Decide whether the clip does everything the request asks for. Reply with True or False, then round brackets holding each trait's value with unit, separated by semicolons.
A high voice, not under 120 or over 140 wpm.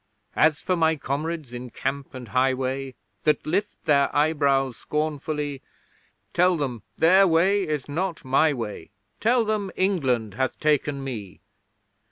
False (145 Hz; 135 wpm)